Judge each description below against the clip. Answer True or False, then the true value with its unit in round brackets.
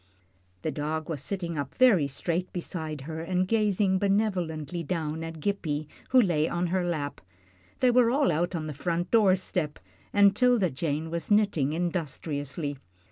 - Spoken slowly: False (160 wpm)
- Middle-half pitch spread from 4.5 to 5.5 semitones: False (4.1 semitones)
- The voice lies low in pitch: False (170 Hz)